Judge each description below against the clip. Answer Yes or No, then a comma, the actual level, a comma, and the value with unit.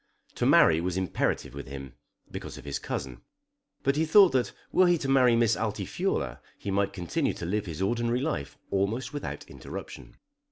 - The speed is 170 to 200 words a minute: Yes, average, 175 wpm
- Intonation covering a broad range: Yes, wide, 7.3 semitones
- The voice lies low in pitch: Yes, low, 105 Hz